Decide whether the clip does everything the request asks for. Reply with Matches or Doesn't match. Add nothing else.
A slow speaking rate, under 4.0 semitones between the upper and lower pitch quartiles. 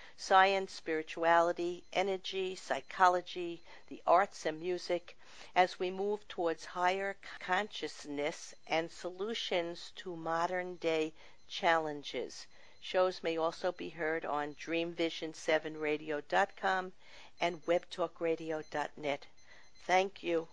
Matches